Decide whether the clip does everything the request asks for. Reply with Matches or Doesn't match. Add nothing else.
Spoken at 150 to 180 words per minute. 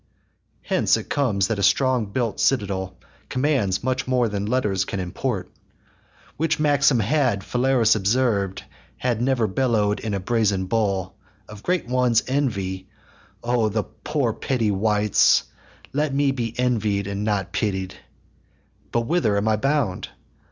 Doesn't match